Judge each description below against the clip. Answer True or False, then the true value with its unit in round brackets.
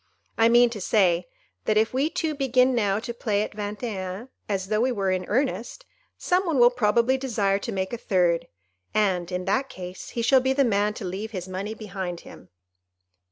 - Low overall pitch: False (215 Hz)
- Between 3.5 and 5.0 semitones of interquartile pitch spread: True (4.3 semitones)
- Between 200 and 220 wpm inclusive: True (205 wpm)